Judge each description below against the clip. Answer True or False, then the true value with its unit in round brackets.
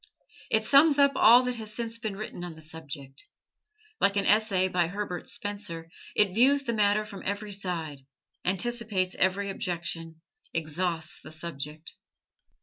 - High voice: True (195 Hz)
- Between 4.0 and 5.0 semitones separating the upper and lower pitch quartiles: True (4.7 semitones)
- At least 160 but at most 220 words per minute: False (145 wpm)